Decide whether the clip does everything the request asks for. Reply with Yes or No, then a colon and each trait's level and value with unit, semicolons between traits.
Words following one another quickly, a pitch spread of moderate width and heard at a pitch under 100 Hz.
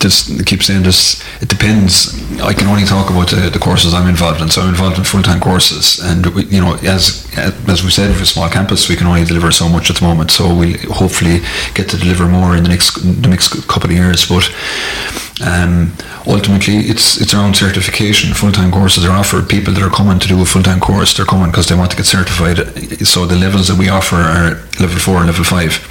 No: fast, 245 wpm; narrow, 2.0 semitones; very low, 90 Hz